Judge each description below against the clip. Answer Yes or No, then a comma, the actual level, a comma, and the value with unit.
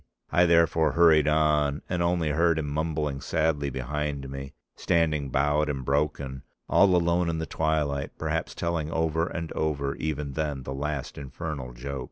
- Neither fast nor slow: Yes, average, 160 wpm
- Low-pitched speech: Yes, very low, 75 Hz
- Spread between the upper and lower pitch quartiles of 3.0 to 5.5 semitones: No, narrow, 2.5 semitones